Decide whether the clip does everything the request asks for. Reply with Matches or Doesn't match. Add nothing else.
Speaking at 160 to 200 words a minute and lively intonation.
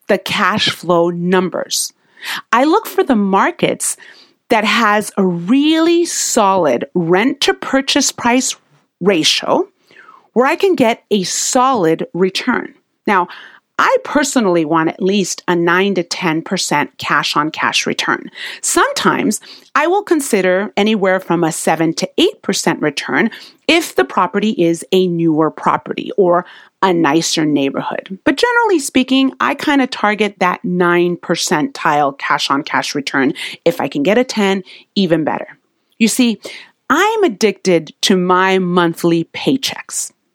Doesn't match